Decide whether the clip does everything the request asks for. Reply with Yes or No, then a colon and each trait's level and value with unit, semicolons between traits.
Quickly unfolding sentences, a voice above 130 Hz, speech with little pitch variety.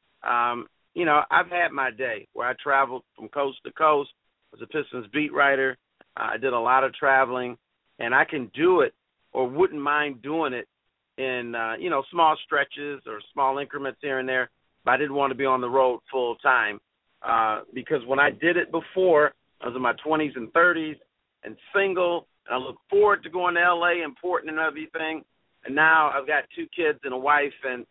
No: fast, 210 wpm; medium, 140 Hz; average, 3.6 semitones